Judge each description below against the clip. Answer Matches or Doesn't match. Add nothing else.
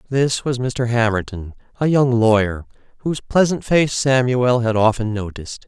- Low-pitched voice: Matches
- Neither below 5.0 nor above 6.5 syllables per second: Doesn't match